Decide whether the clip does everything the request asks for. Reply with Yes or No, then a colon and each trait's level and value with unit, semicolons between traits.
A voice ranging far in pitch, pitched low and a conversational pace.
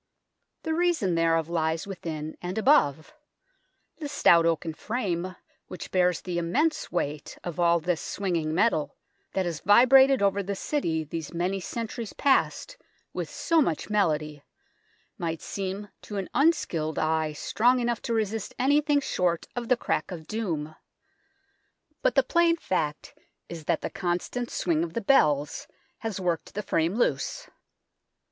No: wide, 6.4 semitones; medium, 185 Hz; average, 145 wpm